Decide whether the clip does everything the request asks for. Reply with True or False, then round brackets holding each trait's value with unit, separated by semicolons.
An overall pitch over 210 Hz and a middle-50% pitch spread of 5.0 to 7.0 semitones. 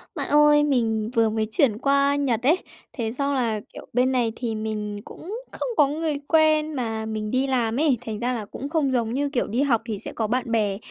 False (245 Hz; 4.3 semitones)